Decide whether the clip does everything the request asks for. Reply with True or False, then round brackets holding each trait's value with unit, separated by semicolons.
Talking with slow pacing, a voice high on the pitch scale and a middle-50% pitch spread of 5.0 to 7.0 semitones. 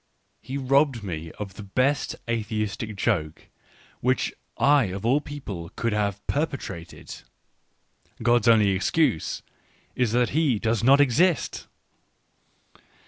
False (120 wpm; 115 Hz; 5.3 semitones)